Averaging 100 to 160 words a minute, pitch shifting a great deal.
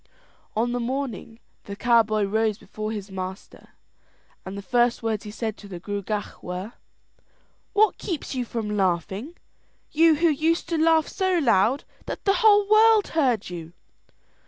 Yes: average, 155 wpm; wide, 7.8 semitones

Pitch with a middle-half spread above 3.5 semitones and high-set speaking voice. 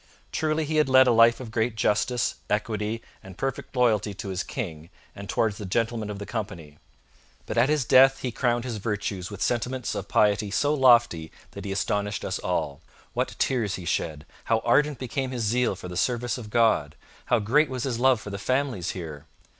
No: average, 4.1 semitones; low, 115 Hz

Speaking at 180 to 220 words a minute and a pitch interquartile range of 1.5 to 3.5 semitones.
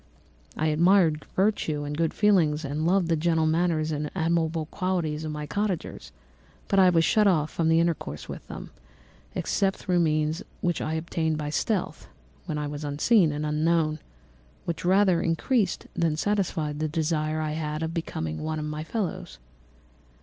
No: average, 165 wpm; narrow, 2.5 semitones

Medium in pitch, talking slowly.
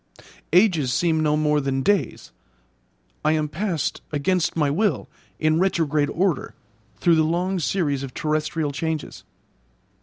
Yes: medium, 155 Hz; slow, 130 wpm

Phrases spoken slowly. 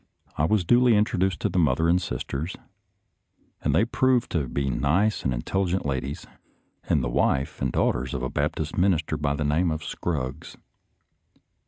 No: average, 165 wpm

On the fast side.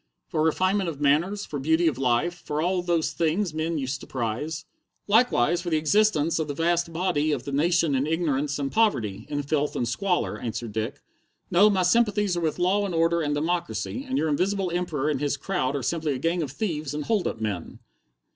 Yes: fast, 210 wpm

